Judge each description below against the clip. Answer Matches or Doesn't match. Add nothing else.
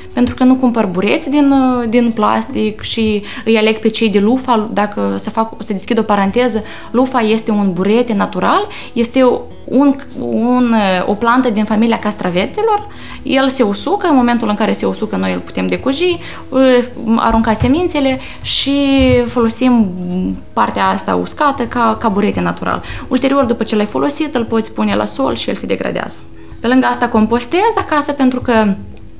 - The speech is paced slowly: Doesn't match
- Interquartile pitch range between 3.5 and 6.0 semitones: Matches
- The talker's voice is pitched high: Matches